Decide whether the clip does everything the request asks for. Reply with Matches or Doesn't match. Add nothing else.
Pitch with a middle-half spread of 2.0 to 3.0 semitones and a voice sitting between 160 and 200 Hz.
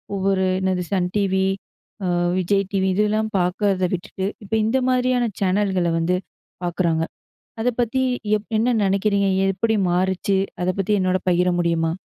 Matches